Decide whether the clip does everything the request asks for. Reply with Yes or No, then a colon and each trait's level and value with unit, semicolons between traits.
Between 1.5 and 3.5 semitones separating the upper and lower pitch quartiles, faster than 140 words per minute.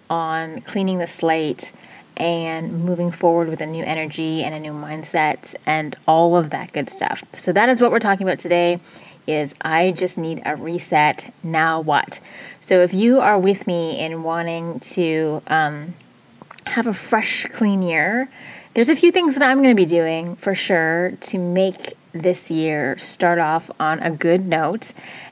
Yes: average, 3.0 semitones; average, 175 wpm